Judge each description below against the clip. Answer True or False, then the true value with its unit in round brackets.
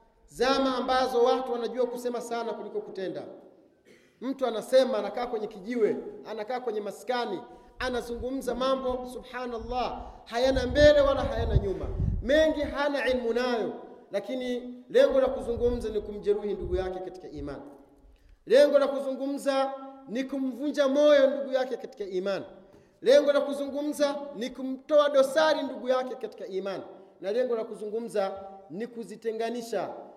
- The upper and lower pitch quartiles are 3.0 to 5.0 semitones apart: True (3.3 semitones)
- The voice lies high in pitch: True (250 Hz)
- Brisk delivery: False (125 wpm)